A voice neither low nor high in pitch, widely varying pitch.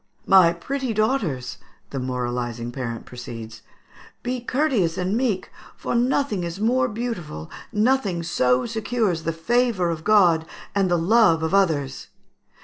Yes: medium, 180 Hz; wide, 8.2 semitones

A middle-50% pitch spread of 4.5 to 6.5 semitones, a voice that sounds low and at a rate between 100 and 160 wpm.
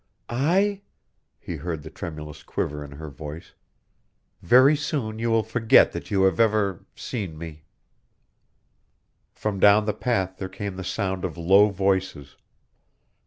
Yes: average, 5.1 semitones; very low, 95 Hz; average, 140 wpm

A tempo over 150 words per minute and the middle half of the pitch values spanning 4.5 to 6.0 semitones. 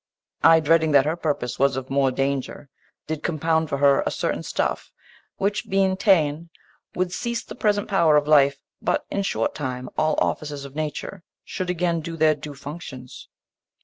No: average, 175 wpm; average, 3.4 semitones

